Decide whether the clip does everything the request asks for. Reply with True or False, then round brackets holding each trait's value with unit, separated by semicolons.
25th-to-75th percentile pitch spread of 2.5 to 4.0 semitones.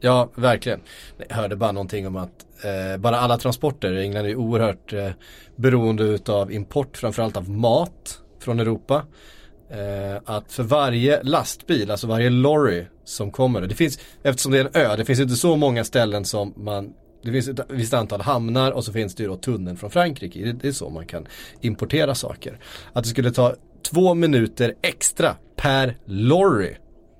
False (4.4 semitones)